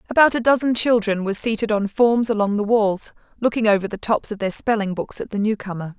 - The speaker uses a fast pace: Yes, fast, 220 wpm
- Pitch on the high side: Yes, high, 215 Hz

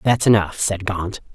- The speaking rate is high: No, average, 180 wpm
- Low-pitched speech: Yes, low, 100 Hz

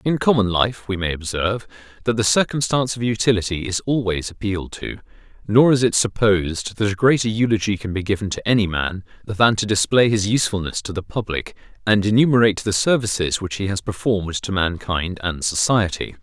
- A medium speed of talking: Yes, average, 180 wpm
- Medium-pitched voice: No, low, 105 Hz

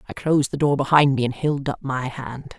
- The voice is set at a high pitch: No, low, 135 Hz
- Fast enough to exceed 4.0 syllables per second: Yes, 5.5 syllables/s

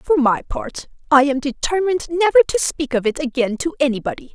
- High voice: Yes, very high, 280 Hz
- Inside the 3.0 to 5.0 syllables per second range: No, 5.6 syllables/s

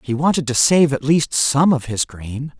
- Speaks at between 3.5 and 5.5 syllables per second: Yes, 4.5 syllables/s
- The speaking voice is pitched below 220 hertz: Yes, medium, 140 Hz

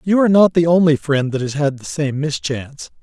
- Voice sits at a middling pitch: Yes, medium, 150 Hz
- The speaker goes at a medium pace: No, fast, 240 wpm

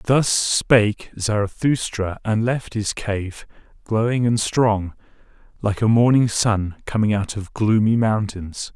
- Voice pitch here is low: Yes, low, 110 Hz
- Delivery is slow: Yes, slow, 130 wpm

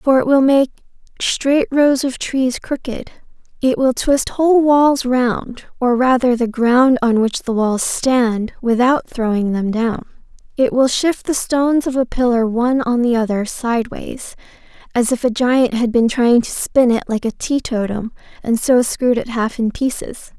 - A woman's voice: Yes, female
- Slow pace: No, average, 175 wpm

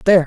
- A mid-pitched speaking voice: Yes, medium, 180 Hz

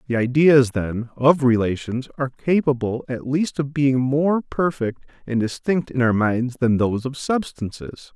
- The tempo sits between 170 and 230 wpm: No, average, 160 wpm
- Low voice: Yes, low, 130 Hz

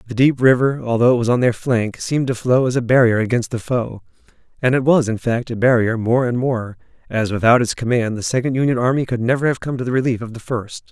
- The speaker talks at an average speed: No, fast, 255 wpm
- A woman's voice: No, male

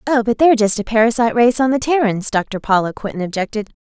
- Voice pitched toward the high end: Yes, high, 225 Hz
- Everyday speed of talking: No, fast, 220 wpm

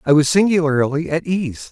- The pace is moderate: Yes, average, 175 wpm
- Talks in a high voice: No, medium, 155 Hz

